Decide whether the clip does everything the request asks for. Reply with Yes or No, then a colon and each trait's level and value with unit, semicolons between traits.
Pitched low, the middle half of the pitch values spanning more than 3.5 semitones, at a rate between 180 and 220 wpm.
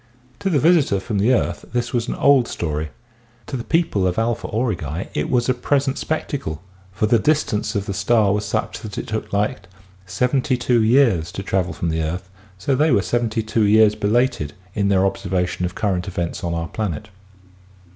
Yes: low, 105 Hz; average, 4.7 semitones; average, 185 wpm